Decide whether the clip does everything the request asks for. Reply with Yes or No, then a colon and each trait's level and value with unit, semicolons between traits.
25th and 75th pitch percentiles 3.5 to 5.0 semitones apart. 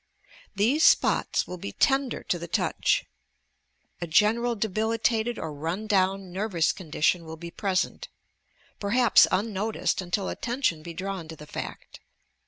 Yes: average, 4.5 semitones